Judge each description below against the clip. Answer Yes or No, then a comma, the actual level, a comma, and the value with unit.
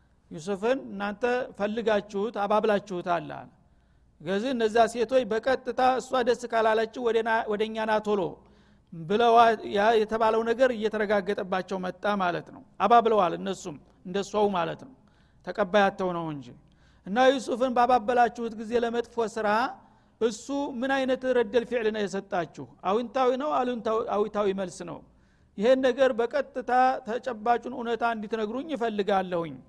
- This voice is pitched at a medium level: No, high, 220 Hz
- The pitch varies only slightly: No, average, 3.5 semitones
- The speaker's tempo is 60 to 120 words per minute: Yes, fast, 110 wpm